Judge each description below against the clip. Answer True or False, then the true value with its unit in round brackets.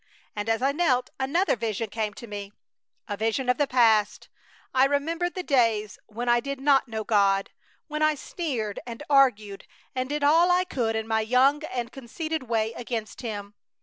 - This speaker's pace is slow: False (180 wpm)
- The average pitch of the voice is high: True (245 Hz)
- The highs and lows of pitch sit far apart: False (4.5 semitones)